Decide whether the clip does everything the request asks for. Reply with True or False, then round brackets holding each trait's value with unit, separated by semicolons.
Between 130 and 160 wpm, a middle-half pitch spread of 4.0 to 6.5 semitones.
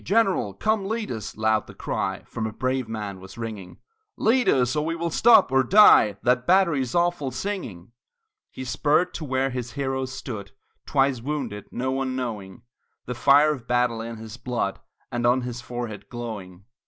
False (175 wpm; 4.6 semitones)